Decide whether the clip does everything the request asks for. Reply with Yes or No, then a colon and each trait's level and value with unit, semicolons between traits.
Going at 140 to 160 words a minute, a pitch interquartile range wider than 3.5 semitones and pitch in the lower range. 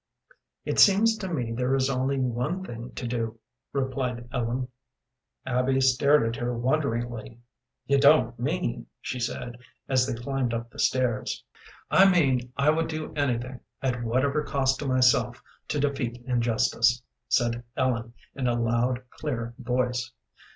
No: average, 150 wpm; narrow, 2.5 semitones; low, 125 Hz